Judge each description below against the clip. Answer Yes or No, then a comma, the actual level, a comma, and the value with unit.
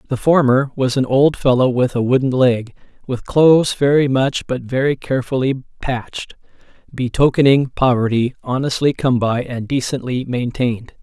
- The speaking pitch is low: Yes, low, 130 Hz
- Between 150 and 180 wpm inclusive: No, average, 140 wpm